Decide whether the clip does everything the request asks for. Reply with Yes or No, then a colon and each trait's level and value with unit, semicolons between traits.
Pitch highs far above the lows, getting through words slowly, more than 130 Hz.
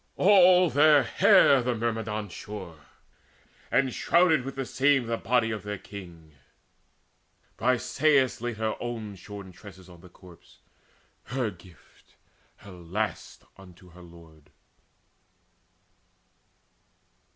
No: wide, 5.8 semitones; slow, 110 wpm; low, 110 Hz